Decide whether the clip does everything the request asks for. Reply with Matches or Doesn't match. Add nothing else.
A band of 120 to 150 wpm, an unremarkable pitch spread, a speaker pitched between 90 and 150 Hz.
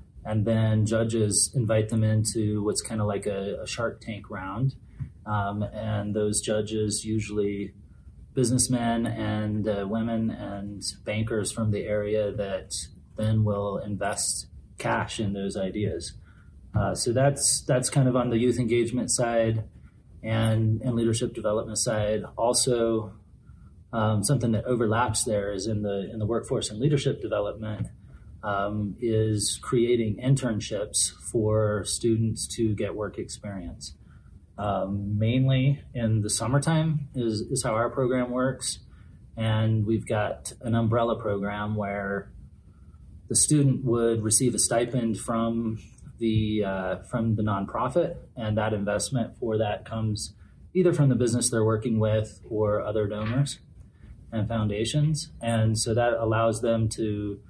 Doesn't match